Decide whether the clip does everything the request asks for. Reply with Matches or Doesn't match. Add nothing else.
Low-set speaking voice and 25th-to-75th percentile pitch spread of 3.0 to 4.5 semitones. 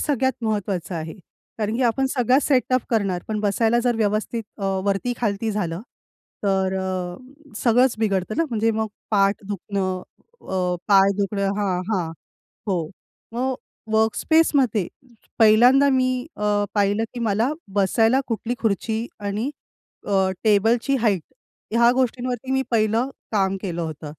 Doesn't match